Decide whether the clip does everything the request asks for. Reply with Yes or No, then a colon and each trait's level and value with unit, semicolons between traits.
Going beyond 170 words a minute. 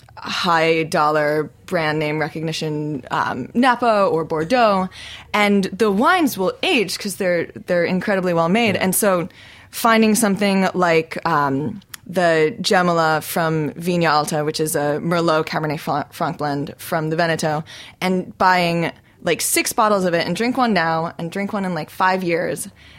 No: average, 155 wpm